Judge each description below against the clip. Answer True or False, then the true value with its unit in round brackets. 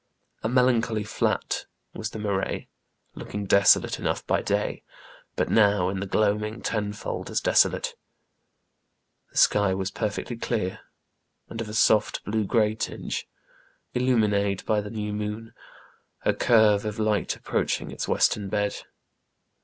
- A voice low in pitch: True (105 Hz)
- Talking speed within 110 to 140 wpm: True (135 wpm)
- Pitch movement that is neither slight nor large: False (1.5 semitones)